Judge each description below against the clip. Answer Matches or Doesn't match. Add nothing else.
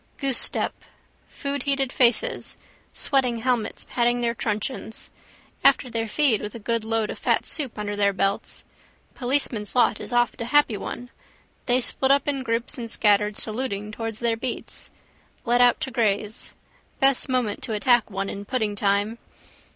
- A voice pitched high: Matches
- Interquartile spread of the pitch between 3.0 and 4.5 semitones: Matches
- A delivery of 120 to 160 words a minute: Matches